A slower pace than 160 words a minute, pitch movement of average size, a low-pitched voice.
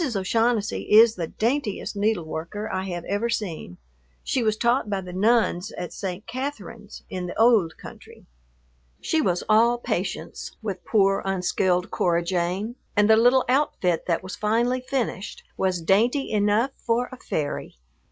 No: average, 150 wpm; average, 4.3 semitones; high, 210 Hz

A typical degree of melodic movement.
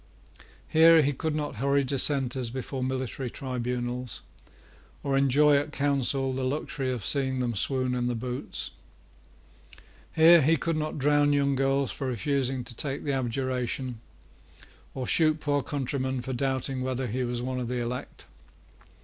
No: narrow, 2.1 semitones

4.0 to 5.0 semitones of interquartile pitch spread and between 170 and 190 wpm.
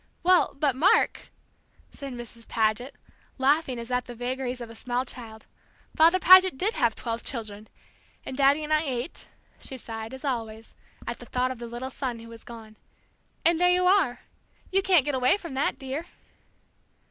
Yes: average, 4.5 semitones; average, 185 wpm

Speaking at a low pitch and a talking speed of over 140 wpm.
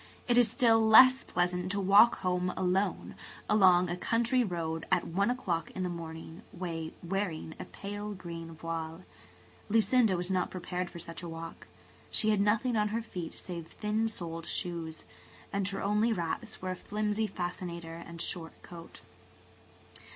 No: medium, 185 Hz; average, 160 wpm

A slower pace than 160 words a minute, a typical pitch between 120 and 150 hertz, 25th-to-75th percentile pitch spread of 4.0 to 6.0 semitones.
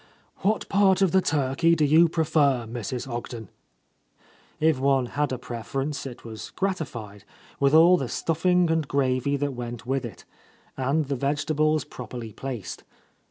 Yes: average, 150 wpm; medium, 140 Hz; average, 4.4 semitones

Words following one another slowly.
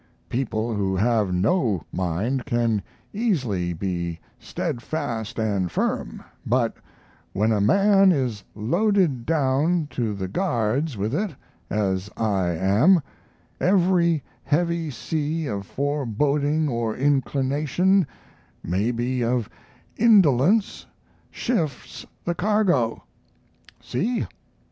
Yes: slow, 100 wpm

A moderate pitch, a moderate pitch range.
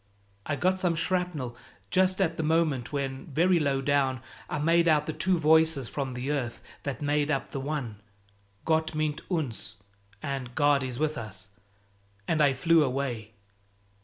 Yes: medium, 145 Hz; average, 3.4 semitones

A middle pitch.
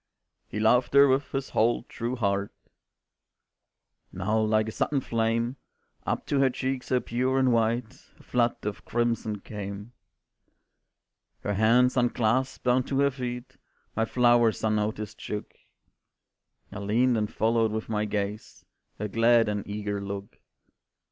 No: low, 115 Hz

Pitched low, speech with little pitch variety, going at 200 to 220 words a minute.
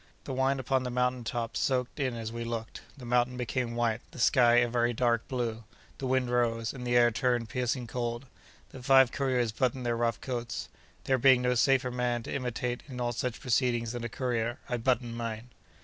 Yes: low, 120 Hz; narrow, 1.4 semitones; fast, 205 wpm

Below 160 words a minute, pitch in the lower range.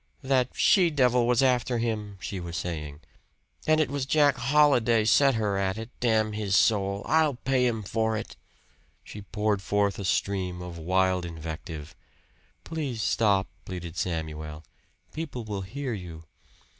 Yes: average, 150 wpm; low, 105 Hz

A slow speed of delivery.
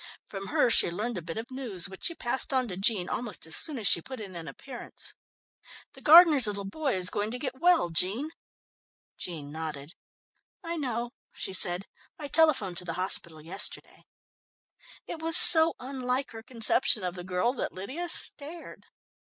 No: average, 175 wpm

